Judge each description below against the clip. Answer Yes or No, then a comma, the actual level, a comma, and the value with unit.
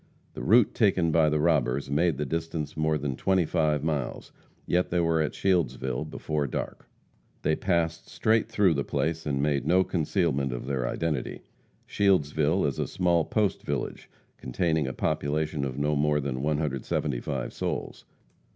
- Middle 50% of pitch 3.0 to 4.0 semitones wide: Yes, average, 3.3 semitones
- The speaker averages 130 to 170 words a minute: Yes, average, 160 wpm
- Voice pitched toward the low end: Yes, very low, 75 Hz